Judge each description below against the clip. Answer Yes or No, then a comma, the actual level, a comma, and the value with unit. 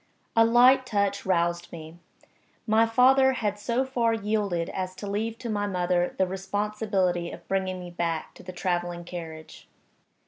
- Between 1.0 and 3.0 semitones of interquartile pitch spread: No, average, 4.3 semitones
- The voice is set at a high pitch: Yes, high, 195 Hz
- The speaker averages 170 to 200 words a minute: No, average, 160 wpm